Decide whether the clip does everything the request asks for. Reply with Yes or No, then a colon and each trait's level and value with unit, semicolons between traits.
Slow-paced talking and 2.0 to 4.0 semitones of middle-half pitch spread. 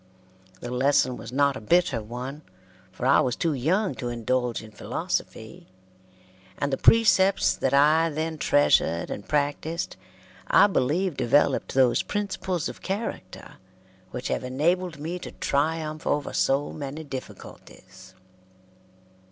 No: slow, 130 wpm; average, 4.5 semitones